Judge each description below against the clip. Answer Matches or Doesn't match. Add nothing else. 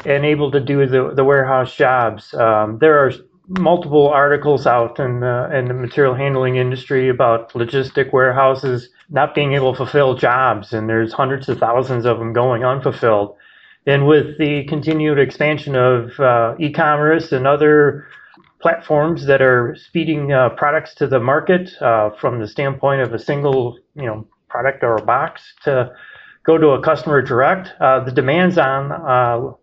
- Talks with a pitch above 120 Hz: Matches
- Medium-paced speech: Matches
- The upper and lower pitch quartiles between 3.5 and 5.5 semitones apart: Doesn't match